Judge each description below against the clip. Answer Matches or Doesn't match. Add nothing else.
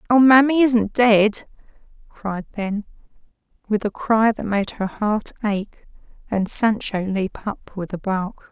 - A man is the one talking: Doesn't match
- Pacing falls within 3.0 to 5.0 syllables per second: Matches